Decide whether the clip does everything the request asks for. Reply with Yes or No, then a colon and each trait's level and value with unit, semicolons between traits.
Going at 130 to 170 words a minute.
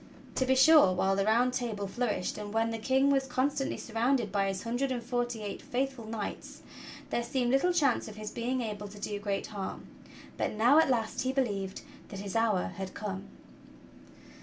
No: average, 195 wpm